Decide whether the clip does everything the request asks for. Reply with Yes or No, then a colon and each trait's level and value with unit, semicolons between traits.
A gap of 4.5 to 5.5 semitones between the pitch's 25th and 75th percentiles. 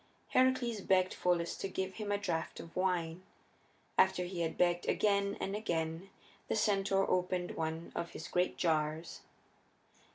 No: average, 2.8 semitones